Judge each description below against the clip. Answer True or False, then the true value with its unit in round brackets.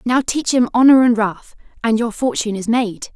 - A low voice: False (235 Hz)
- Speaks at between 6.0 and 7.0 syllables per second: False (5.1 syllables/s)